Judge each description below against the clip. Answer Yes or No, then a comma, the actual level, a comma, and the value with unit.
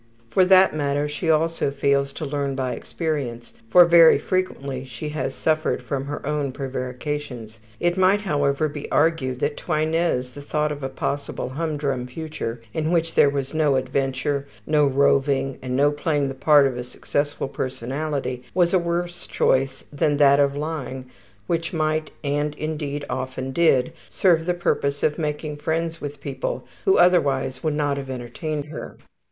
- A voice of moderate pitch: Yes, medium, 145 Hz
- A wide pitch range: No, average, 2.8 semitones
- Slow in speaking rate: No, average, 170 wpm